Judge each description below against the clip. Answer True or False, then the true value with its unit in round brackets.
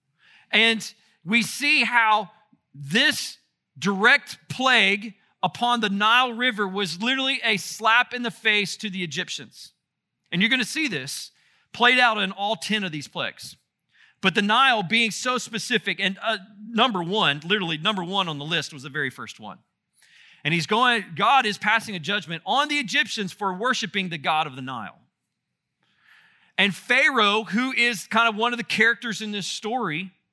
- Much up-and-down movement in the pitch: False (4.2 semitones)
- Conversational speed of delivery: True (170 wpm)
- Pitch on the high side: True (215 Hz)